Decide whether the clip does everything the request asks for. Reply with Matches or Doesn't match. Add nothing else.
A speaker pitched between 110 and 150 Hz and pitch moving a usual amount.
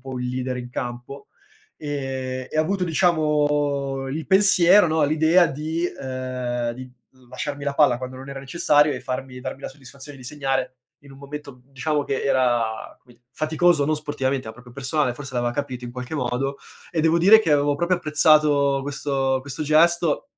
Matches